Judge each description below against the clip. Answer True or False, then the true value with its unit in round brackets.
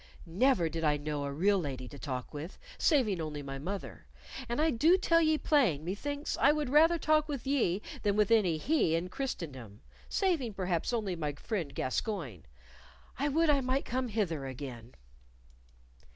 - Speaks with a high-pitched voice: True (195 Hz)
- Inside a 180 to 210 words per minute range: False (170 wpm)